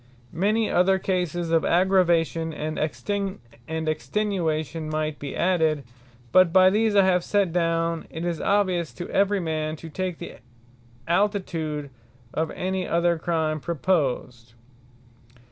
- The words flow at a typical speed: No, slow, 125 wpm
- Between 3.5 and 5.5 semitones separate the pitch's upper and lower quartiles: No, average, 3.0 semitones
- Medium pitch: Yes, medium, 170 Hz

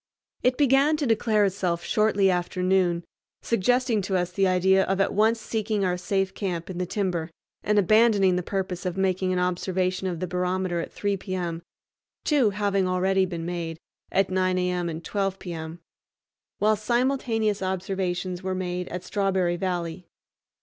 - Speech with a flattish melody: Yes, narrow, 2.2 semitones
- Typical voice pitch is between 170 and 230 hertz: Yes, medium, 185 Hz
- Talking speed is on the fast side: No, average, 160 wpm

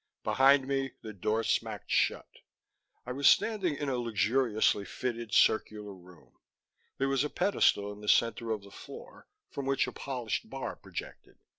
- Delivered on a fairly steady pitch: No, average, 4.3 semitones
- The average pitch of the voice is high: No, low, 120 Hz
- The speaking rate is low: No, average, 160 wpm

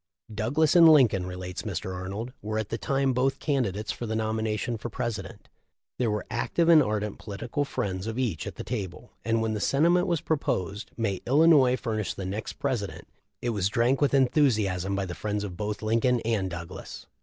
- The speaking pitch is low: Yes, low, 110 Hz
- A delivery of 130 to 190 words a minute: No, average, 200 wpm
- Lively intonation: No, average, 4.3 semitones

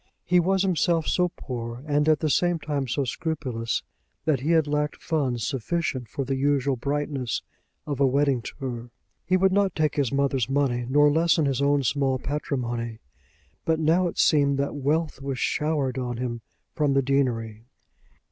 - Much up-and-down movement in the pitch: No, average, 3.3 semitones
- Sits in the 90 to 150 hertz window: Yes, medium, 140 Hz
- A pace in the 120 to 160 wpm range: No, average, 170 wpm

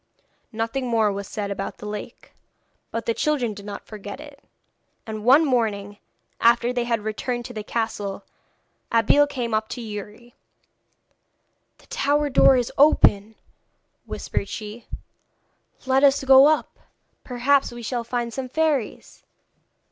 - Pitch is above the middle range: Yes, high, 235 Hz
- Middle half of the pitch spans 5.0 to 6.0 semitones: No, average, 3.8 semitones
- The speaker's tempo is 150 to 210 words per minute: No, average, 140 wpm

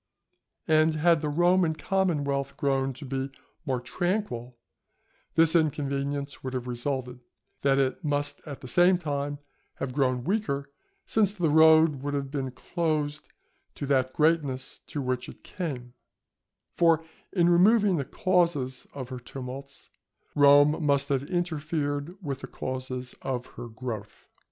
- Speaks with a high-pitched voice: No, medium, 145 Hz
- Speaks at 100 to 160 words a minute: Yes, average, 140 wpm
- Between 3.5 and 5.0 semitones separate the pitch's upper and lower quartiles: Yes, average, 3.8 semitones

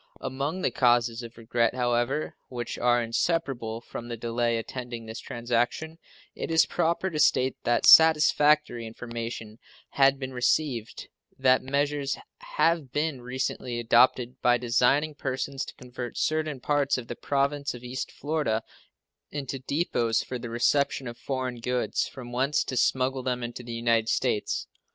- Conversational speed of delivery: Yes, average, 150 wpm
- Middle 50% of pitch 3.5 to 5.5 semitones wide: No, average, 2.9 semitones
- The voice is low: Yes, low, 125 Hz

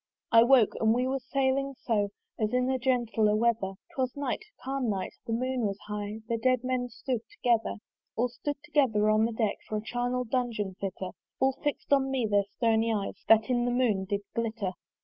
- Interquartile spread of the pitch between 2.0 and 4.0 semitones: Yes, average, 3.1 semitones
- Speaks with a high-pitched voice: Yes, high, 235 Hz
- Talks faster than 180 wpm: Yes, average, 195 wpm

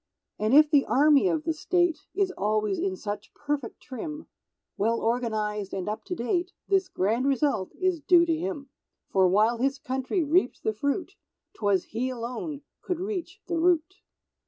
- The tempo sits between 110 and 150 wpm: No, average, 165 wpm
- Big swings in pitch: Yes, wide, 7.6 semitones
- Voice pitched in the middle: No, very high, 275 Hz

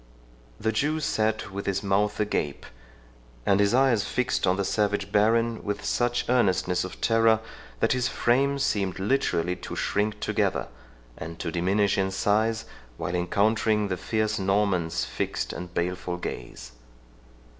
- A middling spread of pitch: Yes, average, 3.0 semitones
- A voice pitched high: No, low, 105 Hz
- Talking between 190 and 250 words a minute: No, average, 145 wpm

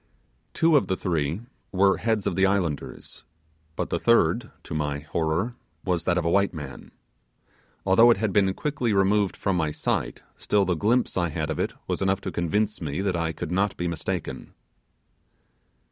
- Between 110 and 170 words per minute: No, average, 180 wpm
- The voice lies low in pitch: Yes, very low, 95 Hz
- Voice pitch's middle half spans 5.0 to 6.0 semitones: No, average, 4.0 semitones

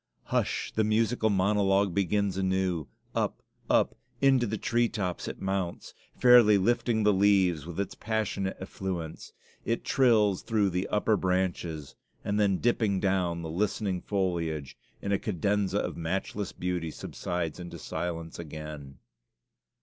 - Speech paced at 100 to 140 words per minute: Yes, slow, 135 wpm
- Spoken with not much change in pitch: No, average, 3.2 semitones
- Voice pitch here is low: Yes, very low, 95 Hz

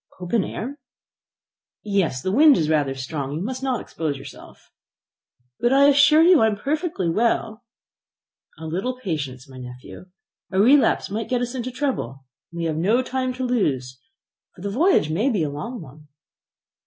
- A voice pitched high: Yes, high, 205 Hz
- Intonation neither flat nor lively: No, wide, 8.9 semitones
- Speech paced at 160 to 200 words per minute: Yes, average, 170 wpm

